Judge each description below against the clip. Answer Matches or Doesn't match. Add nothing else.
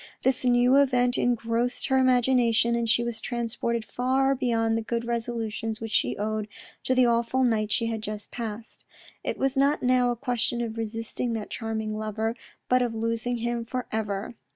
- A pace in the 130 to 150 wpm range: Doesn't match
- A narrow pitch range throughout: Matches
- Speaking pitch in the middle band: Doesn't match